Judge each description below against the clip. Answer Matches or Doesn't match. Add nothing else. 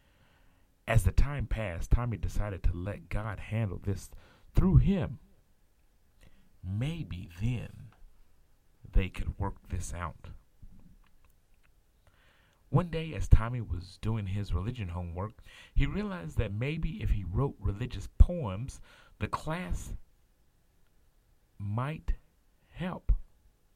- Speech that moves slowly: Matches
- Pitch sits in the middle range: Doesn't match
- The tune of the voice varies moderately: Matches